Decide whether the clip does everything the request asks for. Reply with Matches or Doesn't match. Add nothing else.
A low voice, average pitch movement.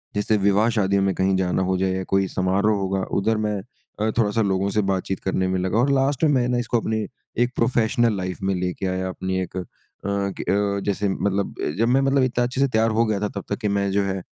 Matches